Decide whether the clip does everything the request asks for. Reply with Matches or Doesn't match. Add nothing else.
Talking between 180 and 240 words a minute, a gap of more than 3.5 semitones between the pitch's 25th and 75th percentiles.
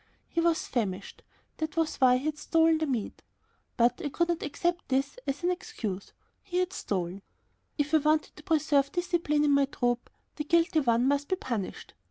Matches